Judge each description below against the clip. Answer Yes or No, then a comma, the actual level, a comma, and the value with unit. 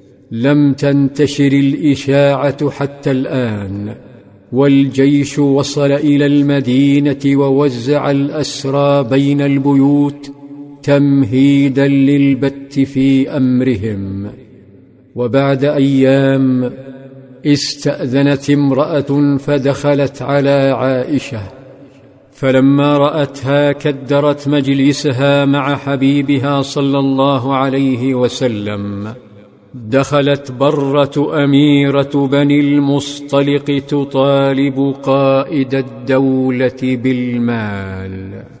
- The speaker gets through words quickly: No, slow, 65 wpm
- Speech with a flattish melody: Yes, narrow, 1.2 semitones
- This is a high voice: No, medium, 140 Hz